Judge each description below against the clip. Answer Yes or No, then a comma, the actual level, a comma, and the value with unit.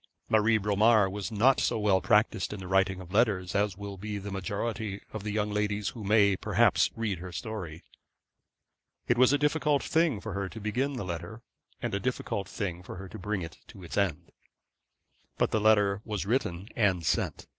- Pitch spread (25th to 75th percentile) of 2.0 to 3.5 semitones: Yes, narrow, 2.4 semitones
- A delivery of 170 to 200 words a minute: Yes, average, 195 wpm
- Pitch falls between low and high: No, low, 105 Hz